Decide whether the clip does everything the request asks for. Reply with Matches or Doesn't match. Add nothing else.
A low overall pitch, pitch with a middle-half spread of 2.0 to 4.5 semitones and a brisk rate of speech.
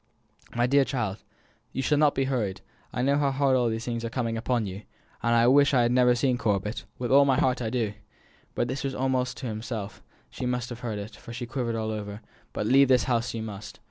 Matches